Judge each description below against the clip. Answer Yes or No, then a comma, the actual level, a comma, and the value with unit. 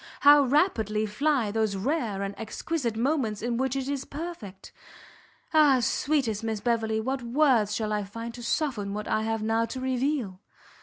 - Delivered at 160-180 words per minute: Yes, average, 165 wpm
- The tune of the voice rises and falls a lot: No, average, 4.3 semitones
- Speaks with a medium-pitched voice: No, high, 230 Hz